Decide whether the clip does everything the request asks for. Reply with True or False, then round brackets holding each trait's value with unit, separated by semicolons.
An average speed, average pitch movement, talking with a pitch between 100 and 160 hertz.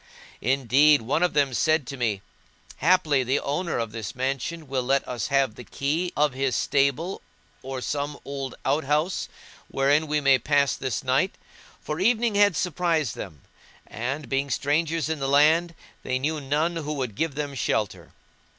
True (165 wpm; 3.0 semitones; 140 Hz)